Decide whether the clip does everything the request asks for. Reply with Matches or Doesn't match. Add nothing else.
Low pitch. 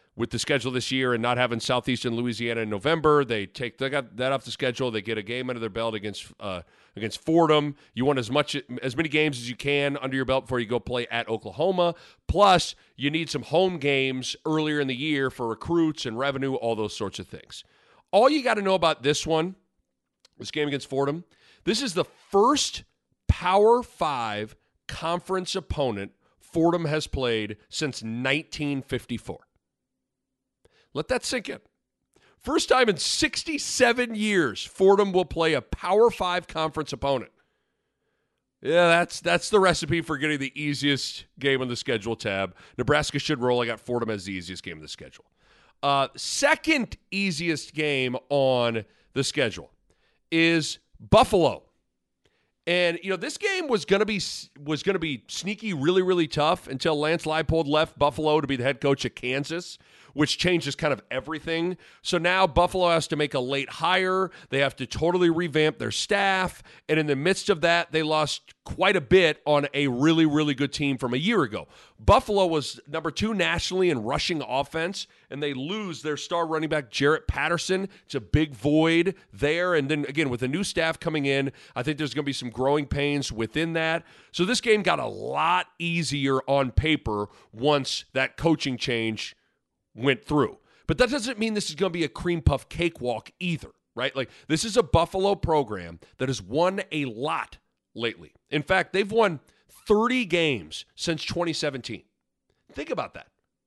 Doesn't match